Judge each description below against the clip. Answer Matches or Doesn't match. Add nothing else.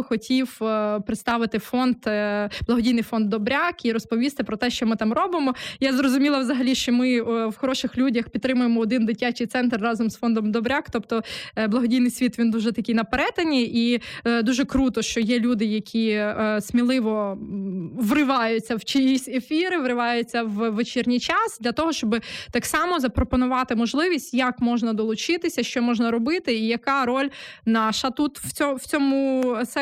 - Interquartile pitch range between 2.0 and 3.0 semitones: Matches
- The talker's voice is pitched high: Matches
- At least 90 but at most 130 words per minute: Doesn't match